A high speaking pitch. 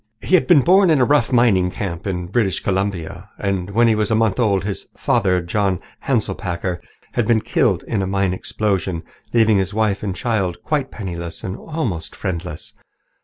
No: low, 100 Hz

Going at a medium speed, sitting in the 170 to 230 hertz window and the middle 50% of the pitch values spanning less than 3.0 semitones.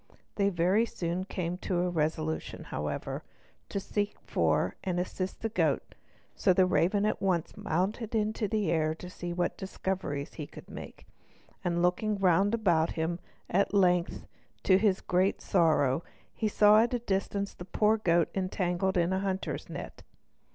Yes: average, 160 wpm; medium, 185 Hz; narrow, 2.6 semitones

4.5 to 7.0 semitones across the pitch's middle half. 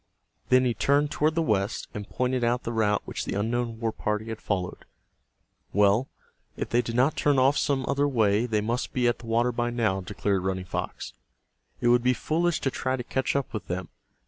No: average, 3.6 semitones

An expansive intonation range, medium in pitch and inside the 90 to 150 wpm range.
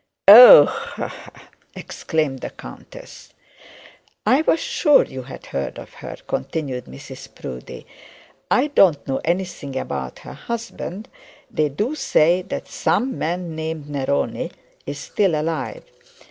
Yes: wide, 7.5 semitones; medium, 160 Hz; slow, 135 wpm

